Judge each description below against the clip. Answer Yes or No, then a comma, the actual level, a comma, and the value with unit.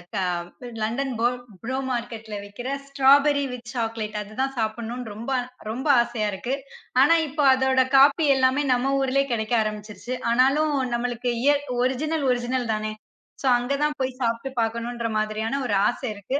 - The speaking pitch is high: Yes, high, 245 Hz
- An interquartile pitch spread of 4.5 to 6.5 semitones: No, average, 3.3 semitones